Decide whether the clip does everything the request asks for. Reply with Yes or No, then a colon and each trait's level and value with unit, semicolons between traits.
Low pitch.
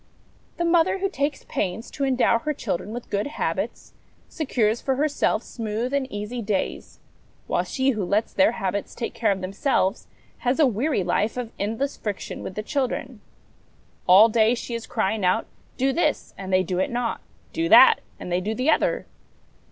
No: high, 230 Hz